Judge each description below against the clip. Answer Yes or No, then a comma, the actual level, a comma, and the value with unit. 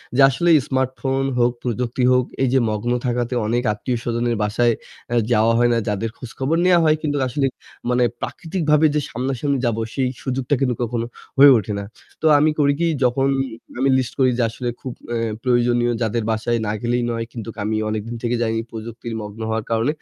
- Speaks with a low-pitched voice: Yes, low, 120 Hz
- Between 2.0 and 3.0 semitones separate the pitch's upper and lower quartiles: Yes, narrow, 2.5 semitones